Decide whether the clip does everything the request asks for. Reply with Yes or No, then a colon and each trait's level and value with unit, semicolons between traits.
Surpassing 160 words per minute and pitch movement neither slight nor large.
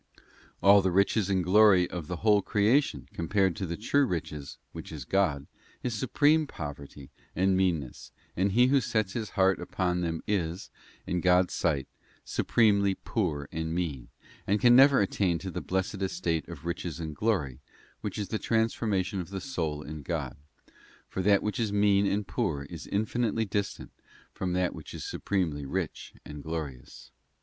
Yes: average, 170 wpm; average, 4.2 semitones